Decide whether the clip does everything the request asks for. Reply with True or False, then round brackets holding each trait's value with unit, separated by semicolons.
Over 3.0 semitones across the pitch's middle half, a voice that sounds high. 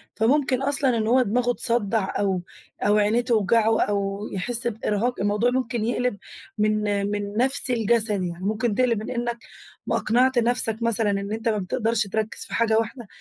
False (2.7 semitones; 225 Hz)